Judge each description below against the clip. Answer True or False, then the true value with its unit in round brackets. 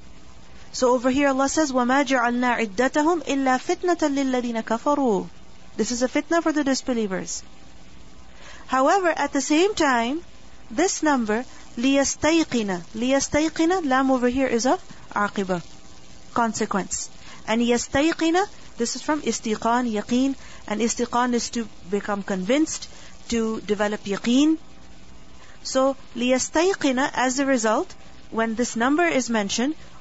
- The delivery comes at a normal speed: False (105 wpm)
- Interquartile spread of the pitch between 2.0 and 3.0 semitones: False (4.4 semitones)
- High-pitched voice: True (250 Hz)